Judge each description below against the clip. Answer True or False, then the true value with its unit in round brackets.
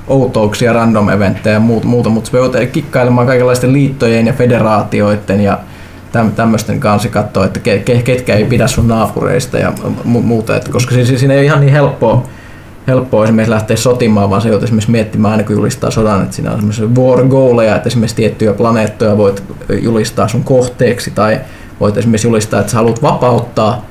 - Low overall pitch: True (115 Hz)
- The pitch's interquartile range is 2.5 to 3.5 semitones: True (2.9 semitones)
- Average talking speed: False (165 wpm)